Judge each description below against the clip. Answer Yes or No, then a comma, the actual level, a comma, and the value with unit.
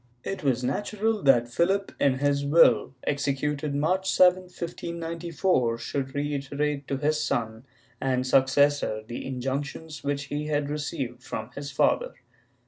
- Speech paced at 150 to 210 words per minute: No, slow, 135 wpm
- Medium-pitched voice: Yes, medium, 145 Hz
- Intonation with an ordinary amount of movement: Yes, average, 3.5 semitones